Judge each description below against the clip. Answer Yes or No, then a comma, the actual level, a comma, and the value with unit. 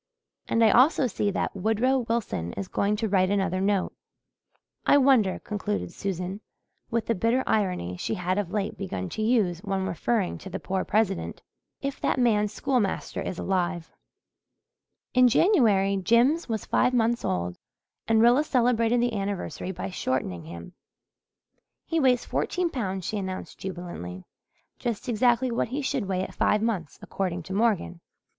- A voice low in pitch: No, high, 205 Hz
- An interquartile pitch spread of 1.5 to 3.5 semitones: No, average, 4.2 semitones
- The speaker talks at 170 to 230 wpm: No, average, 155 wpm